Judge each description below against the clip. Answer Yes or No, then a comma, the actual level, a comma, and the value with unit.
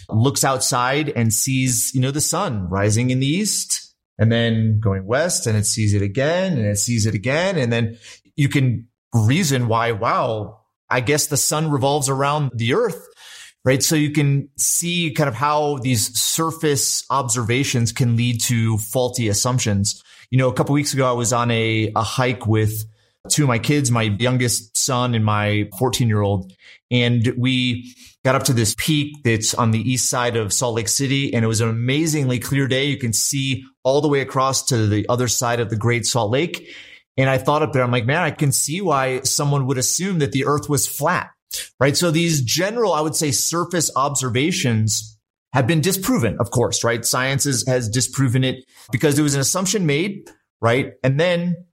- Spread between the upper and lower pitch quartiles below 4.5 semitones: Yes, average, 3.7 semitones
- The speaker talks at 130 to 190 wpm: No, average, 200 wpm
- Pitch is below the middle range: Yes, low, 130 Hz